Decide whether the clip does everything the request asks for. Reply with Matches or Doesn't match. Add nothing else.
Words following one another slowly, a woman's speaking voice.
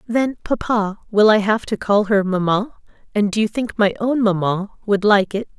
Doesn't match